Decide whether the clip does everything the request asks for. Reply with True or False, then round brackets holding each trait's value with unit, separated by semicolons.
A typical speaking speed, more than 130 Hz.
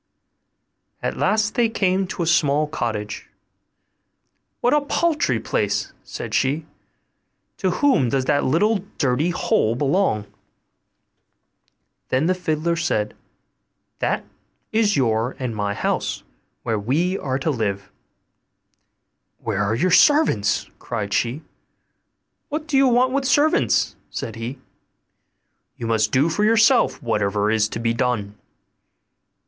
False (125 wpm; 140 Hz)